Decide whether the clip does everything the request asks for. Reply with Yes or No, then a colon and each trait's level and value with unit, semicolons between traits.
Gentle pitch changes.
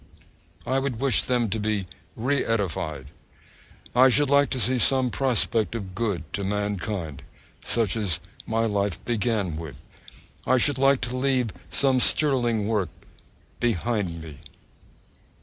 No: average, 4.6 semitones